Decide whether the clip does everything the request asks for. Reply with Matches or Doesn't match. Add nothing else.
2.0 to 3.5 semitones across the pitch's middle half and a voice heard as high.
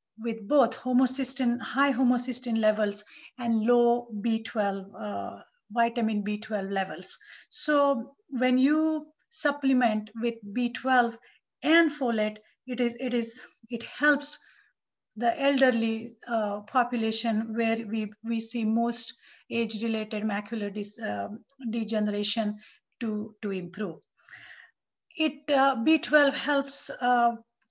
Matches